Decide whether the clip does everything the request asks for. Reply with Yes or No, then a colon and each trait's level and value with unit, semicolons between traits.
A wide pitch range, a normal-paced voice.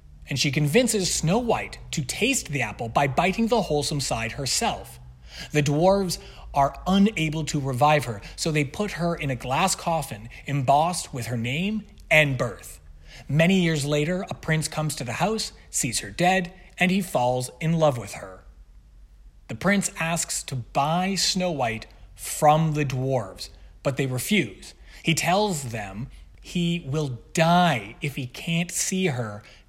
Yes: wide, 6.1 semitones; average, 160 wpm